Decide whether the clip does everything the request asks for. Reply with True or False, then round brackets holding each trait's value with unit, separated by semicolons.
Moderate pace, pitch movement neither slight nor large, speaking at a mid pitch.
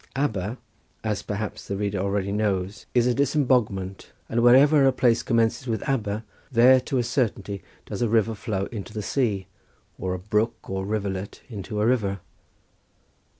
False (160 wpm; 3.6 semitones; 110 Hz)